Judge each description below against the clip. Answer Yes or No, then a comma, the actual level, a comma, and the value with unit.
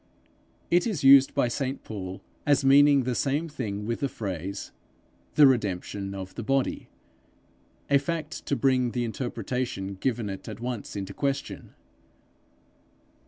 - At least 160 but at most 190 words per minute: No, average, 140 wpm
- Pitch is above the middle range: No, low, 125 Hz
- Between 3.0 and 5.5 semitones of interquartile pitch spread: Yes, average, 5.2 semitones